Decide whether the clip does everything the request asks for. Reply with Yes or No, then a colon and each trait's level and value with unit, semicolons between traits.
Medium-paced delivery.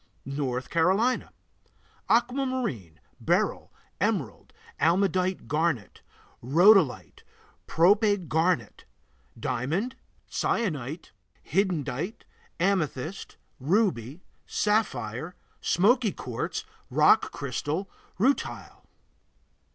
No: slow, 65 wpm